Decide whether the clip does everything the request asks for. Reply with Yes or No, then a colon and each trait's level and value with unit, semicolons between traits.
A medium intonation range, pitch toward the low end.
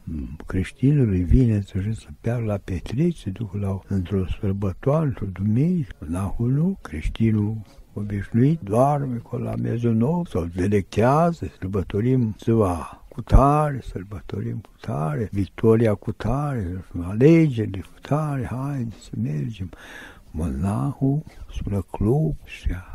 Yes: average, 5.0 semitones; low, 110 Hz